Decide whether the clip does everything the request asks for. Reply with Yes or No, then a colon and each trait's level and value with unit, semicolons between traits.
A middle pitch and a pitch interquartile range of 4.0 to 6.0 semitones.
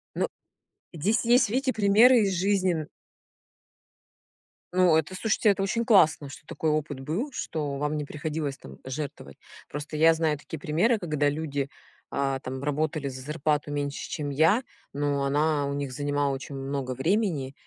Yes: medium, 150 Hz; average, 4.5 semitones